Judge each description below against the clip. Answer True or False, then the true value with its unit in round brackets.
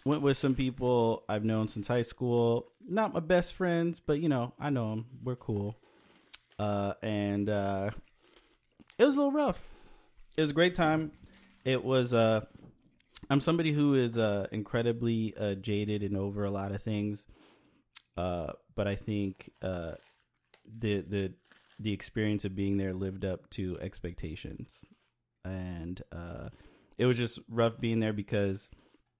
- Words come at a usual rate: True (155 wpm)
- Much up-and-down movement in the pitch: False (4.3 semitones)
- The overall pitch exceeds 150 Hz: False (110 Hz)